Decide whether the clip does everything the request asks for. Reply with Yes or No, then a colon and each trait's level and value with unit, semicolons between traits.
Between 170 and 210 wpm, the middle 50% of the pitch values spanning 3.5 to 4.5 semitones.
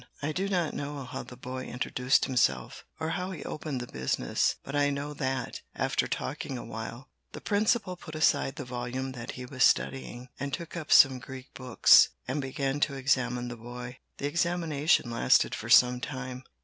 No: average, 180 wpm; average, 2.9 semitones